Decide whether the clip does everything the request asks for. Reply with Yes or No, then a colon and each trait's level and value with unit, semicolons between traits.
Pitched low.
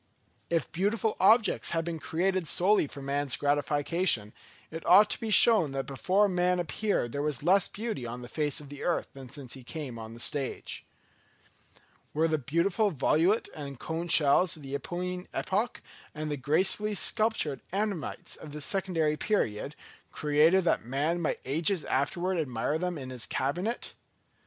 No: medium, 160 Hz